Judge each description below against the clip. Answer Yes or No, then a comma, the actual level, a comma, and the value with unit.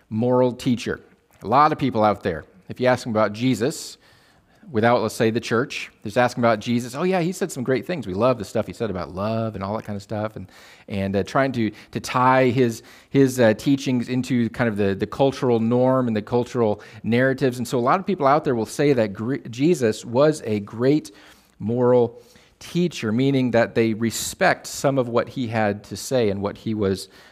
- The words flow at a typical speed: No, fast, 215 wpm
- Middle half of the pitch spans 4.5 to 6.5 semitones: No, average, 3.2 semitones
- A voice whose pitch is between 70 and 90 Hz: No, low, 120 Hz